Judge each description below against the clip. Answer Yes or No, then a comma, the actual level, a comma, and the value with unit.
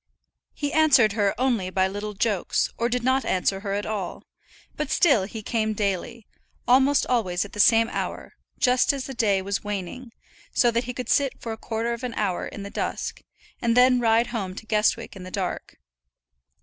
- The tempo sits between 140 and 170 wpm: No, average, 195 wpm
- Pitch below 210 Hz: No, high, 225 Hz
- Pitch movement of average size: Yes, average, 3.6 semitones